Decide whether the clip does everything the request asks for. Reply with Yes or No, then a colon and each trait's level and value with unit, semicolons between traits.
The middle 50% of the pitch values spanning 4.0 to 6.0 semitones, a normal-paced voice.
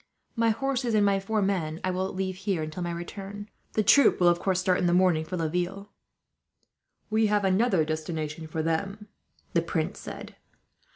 No: average, 3.2 semitones; average, 180 wpm